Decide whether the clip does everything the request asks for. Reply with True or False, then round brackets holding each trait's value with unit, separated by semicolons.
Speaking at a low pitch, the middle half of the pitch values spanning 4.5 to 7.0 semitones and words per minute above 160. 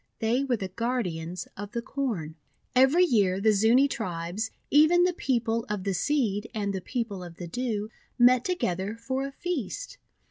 False (225 Hz; 5.3 semitones; 175 wpm)